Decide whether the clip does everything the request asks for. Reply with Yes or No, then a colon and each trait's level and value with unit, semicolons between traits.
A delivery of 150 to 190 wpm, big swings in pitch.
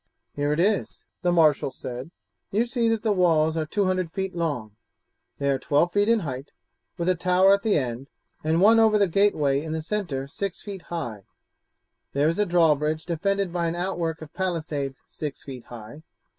No: average, 185 wpm; average, 4.9 semitones